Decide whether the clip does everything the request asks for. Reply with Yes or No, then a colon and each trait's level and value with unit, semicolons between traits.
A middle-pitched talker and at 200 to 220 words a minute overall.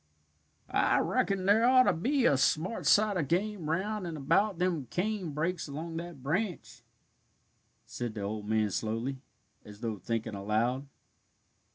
No: medium, 160 Hz; average, 150 wpm